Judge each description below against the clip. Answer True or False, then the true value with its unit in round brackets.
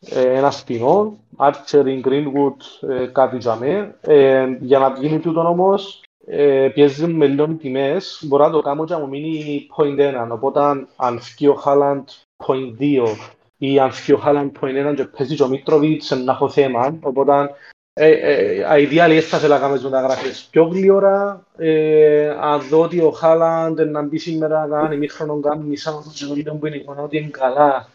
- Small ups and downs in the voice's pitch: True (2.3 semitones)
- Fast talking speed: False (150 wpm)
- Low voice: False (145 Hz)